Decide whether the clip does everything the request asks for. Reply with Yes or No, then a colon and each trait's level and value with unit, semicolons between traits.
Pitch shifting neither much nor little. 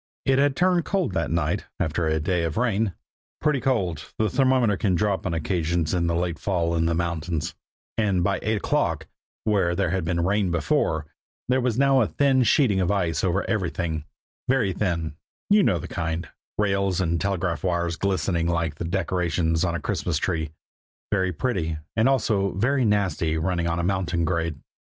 Yes: average, 4.0 semitones